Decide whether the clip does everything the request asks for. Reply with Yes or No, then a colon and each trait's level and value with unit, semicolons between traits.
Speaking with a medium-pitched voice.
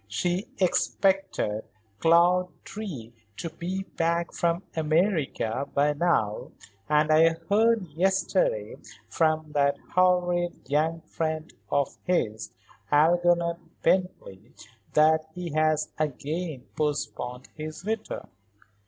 Yes: medium, 165 Hz